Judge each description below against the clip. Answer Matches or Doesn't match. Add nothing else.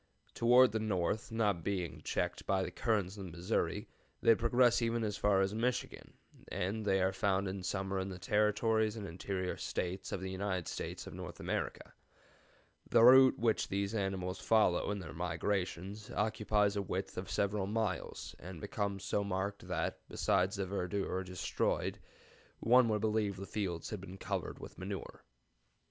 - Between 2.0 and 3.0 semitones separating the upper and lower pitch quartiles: Matches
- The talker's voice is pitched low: Matches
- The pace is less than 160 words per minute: Doesn't match